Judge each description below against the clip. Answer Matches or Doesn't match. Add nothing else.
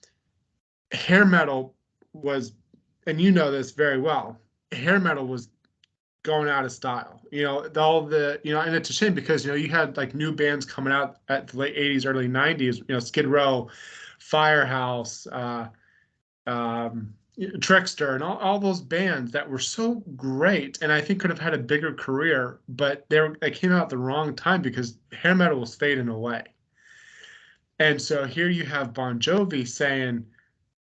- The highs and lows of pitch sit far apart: Doesn't match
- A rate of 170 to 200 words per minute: Matches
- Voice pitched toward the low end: Doesn't match